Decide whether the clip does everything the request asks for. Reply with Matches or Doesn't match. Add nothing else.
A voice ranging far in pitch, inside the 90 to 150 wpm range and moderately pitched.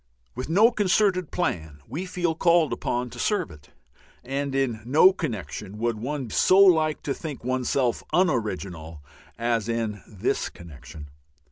Doesn't match